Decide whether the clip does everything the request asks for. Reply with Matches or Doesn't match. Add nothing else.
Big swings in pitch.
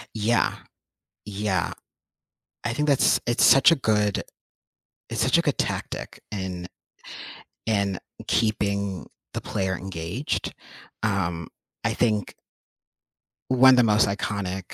Doesn't match